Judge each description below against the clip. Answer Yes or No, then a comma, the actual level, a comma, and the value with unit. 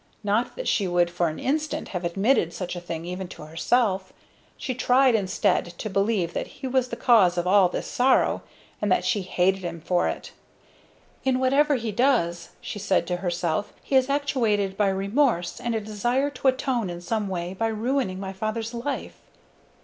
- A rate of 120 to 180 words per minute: No, average, 190 wpm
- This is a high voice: Yes, high, 205 Hz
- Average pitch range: No, wide, 5.8 semitones